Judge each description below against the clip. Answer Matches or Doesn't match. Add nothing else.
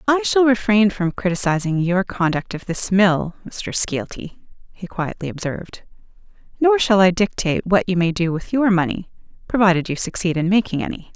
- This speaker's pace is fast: Doesn't match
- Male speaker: Doesn't match